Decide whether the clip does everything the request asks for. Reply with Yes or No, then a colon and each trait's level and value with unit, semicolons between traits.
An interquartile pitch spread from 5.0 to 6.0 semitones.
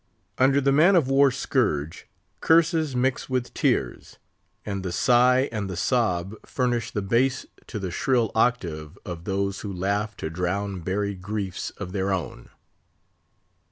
Yes: wide, 5.4 semitones